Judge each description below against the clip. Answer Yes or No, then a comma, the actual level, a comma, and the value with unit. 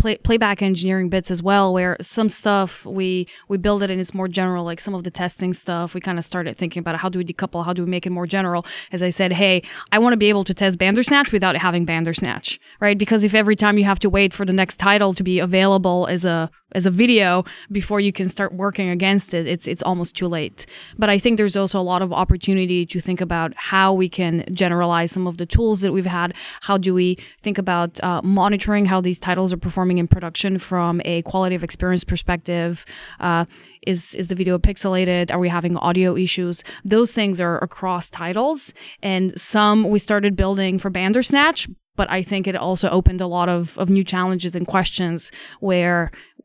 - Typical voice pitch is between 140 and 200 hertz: Yes, medium, 185 Hz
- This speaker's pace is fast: Yes, fast, 220 wpm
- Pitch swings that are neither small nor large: No, narrow, 1.9 semitones